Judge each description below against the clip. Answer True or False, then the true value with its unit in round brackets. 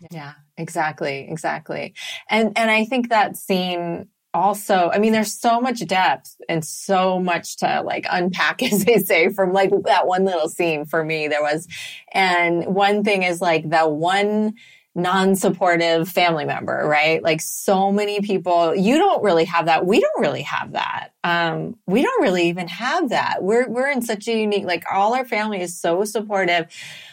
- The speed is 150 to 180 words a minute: True (175 wpm)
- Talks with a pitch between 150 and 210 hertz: True (185 Hz)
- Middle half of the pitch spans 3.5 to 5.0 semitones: True (3.9 semitones)